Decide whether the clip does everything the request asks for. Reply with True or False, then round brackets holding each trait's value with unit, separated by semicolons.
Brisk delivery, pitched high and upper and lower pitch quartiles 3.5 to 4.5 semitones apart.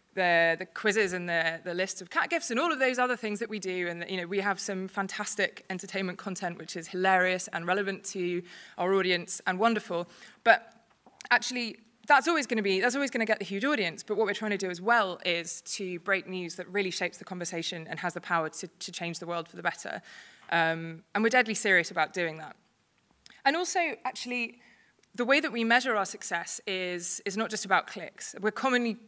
True (225 wpm; 195 Hz; 4.1 semitones)